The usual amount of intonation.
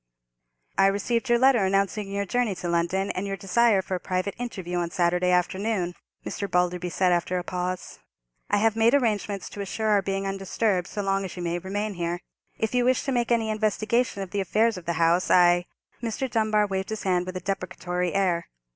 Yes: average, 3.3 semitones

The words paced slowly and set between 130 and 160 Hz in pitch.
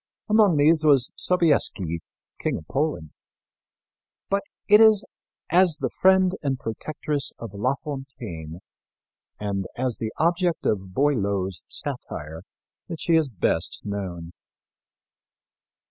Yes: slow, 115 wpm; low, 135 Hz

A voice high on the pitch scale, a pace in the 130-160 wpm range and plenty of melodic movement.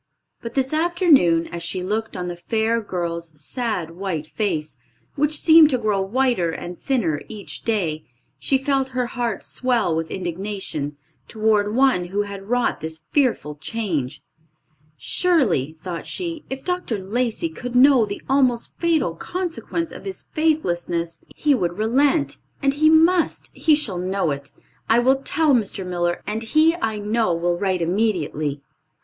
Yes: high, 215 Hz; average, 155 wpm; wide, 7.6 semitones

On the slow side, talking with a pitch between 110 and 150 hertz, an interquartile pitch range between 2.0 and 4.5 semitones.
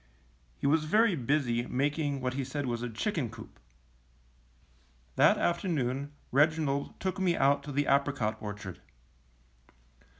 Yes: slow, 130 wpm; medium, 140 Hz; average, 3.7 semitones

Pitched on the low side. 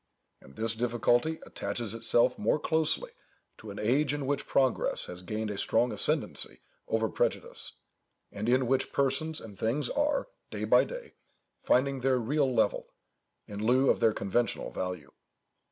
Yes: low, 120 Hz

